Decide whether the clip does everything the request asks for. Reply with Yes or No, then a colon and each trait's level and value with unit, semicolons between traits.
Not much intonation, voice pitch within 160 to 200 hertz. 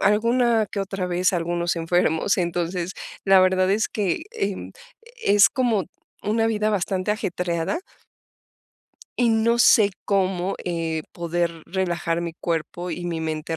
No: average, 3.3 semitones; medium, 185 Hz